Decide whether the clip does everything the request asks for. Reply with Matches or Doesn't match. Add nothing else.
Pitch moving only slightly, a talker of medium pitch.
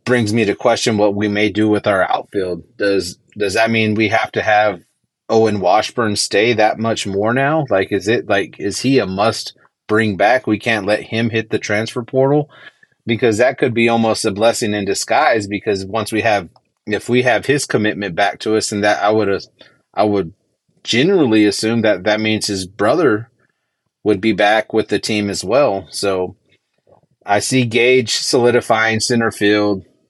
Doesn't match